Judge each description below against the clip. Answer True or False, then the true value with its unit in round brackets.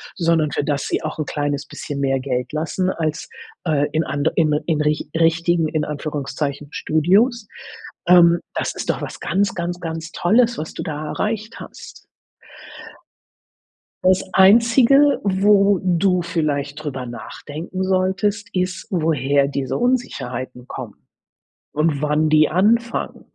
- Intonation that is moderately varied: True (4.3 semitones)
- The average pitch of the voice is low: False (165 Hz)